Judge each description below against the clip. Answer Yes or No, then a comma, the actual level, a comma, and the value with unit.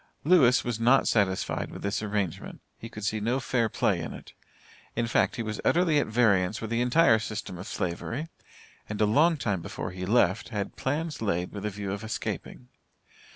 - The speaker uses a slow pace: No, average, 195 wpm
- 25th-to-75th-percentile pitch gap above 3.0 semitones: Yes, average, 3.6 semitones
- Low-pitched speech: Yes, low, 110 Hz